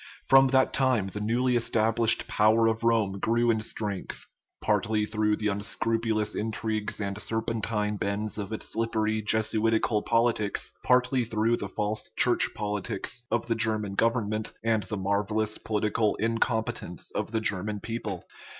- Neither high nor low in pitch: No, low, 110 Hz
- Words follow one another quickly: No, average, 140 wpm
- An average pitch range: No, narrow, 1.5 semitones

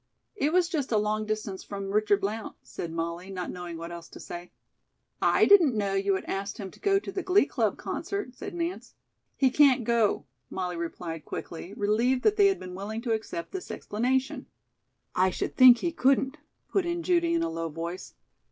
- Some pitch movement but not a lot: No, wide, 8.4 semitones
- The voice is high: Yes, high, 215 Hz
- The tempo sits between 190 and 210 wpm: Yes, average, 200 wpm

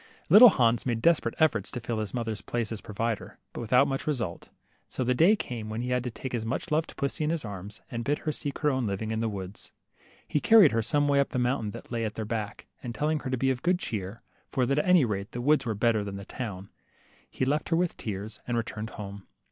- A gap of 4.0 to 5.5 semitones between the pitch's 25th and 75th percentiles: Yes, average, 4.6 semitones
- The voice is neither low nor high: No, low, 120 Hz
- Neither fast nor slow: No, fast, 260 wpm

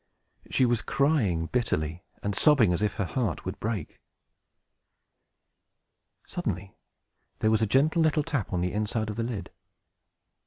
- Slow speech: No, average, 145 wpm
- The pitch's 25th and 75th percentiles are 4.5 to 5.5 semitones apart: Yes, average, 5.1 semitones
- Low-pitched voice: Yes, low, 110 Hz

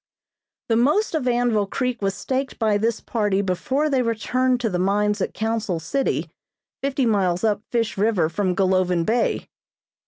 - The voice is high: Yes, high, 220 Hz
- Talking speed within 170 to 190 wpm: No, average, 160 wpm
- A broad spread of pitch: No, average, 4.2 semitones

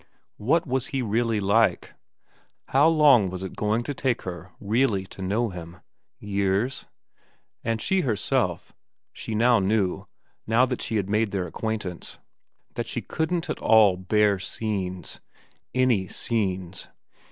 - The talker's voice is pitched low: Yes, low, 105 Hz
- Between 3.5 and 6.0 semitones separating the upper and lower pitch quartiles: Yes, average, 4.2 semitones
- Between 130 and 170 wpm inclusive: Yes, average, 140 wpm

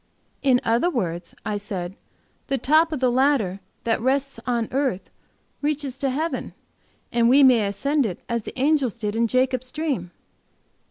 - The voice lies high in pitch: Yes, very high, 255 Hz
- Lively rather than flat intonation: No, average, 4.0 semitones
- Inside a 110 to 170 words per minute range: Yes, average, 160 wpm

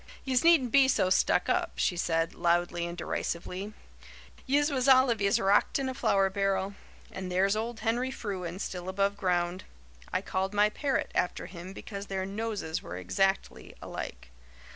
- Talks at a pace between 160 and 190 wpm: Yes, average, 165 wpm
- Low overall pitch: No, high, 195 Hz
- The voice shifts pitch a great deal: No, average, 4.0 semitones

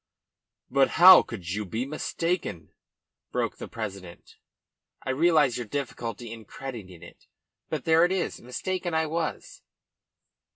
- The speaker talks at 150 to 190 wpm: No, slow, 135 wpm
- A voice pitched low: Yes, low, 130 Hz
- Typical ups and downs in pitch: No, wide, 6.9 semitones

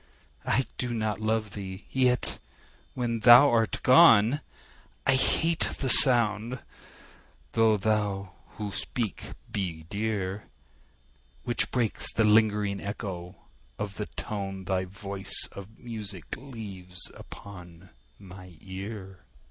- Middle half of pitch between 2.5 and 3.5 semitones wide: Yes, average, 3.1 semitones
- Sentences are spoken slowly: Yes, slow, 110 wpm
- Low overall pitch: Yes, low, 105 Hz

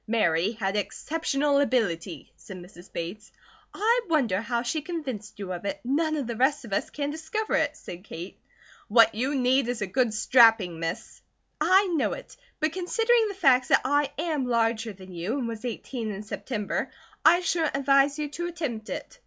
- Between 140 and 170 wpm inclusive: No, average, 185 wpm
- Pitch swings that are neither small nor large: No, wide, 6.2 semitones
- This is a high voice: Yes, very high, 250 Hz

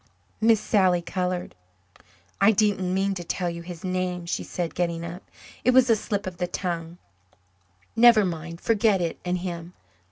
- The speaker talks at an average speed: Yes, average, 165 wpm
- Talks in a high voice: No, medium, 180 Hz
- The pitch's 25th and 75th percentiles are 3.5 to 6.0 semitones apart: No, average, 2.7 semitones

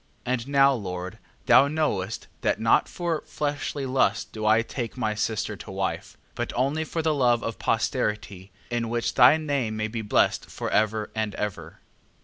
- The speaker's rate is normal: Yes, average, 175 wpm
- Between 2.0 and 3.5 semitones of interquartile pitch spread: No, average, 4.4 semitones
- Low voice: Yes, low, 115 Hz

